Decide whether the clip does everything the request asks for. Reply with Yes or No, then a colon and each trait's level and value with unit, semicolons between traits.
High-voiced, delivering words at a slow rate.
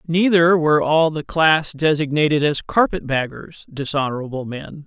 No: medium, 155 Hz; slow, 125 wpm